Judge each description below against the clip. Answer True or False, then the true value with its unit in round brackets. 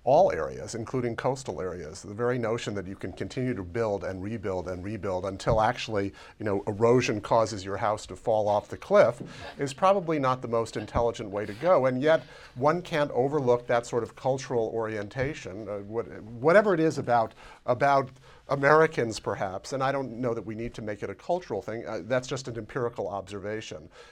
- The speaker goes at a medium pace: True (195 wpm)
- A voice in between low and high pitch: False (115 Hz)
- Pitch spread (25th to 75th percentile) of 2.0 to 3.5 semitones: False (4.0 semitones)